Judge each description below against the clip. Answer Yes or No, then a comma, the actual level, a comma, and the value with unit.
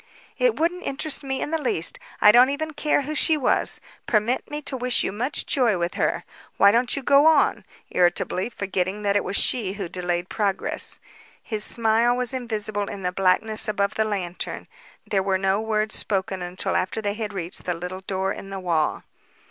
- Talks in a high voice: Yes, high, 210 Hz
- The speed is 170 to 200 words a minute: Yes, average, 195 wpm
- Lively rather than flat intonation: No, average, 4.8 semitones